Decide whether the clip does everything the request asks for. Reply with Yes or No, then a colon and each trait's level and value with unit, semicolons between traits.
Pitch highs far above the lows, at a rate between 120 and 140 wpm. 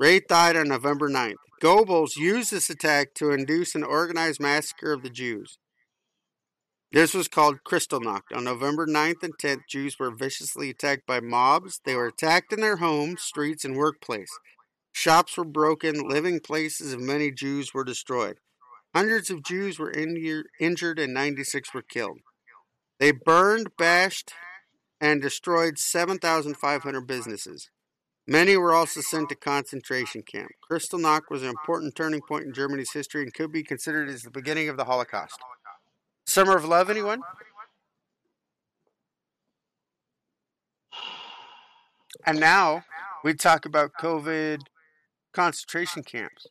No: average, 3.2 semitones; slow, 135 wpm